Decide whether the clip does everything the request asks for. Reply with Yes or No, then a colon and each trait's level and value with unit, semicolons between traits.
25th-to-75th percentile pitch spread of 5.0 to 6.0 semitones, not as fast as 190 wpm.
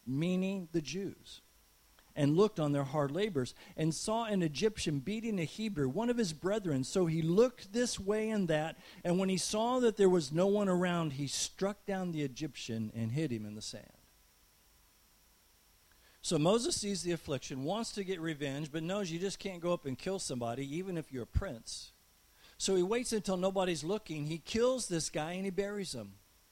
No: wide, 5.5 semitones; average, 195 wpm